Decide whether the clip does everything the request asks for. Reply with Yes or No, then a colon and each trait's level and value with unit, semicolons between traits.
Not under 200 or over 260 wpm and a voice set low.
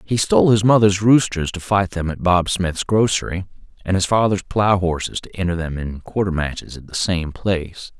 Yes: fast, 205 wpm; very low, 90 Hz